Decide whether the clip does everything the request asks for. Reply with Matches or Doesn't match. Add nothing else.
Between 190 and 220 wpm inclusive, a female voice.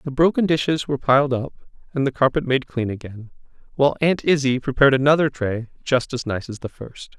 Doesn't match